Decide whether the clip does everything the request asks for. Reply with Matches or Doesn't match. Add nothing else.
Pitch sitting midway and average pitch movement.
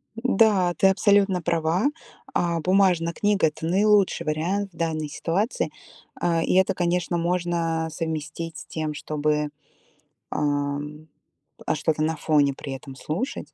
Matches